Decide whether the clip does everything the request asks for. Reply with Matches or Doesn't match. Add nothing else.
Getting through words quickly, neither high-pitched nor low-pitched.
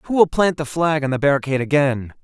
Matches